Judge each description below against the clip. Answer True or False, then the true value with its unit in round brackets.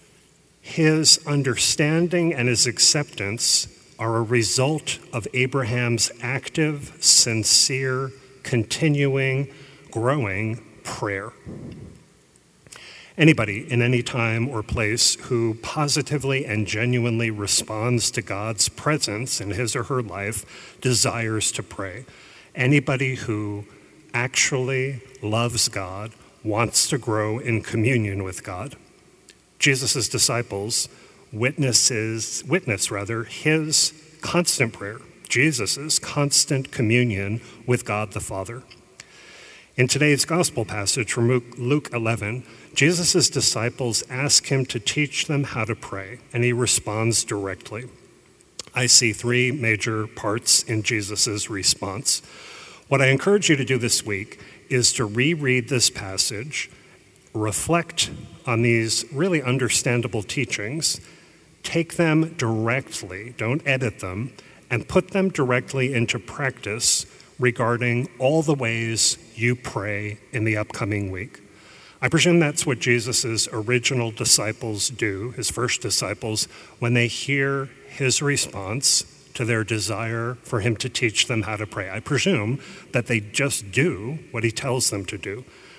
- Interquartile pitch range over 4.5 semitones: False (3.6 semitones)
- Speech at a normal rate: False (120 wpm)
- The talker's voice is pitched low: True (120 Hz)